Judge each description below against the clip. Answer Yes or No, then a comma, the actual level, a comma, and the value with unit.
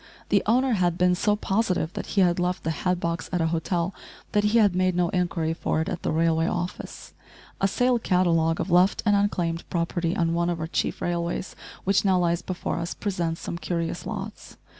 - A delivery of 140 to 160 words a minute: No, fast, 205 wpm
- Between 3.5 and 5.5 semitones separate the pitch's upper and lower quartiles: No, narrow, 2.4 semitones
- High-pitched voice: No, medium, 180 Hz